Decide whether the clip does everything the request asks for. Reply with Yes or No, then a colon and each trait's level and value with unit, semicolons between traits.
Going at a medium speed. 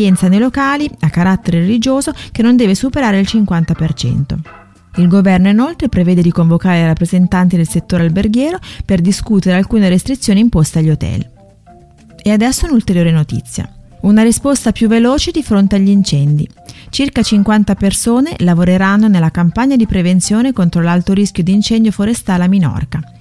Yes: average, 145 wpm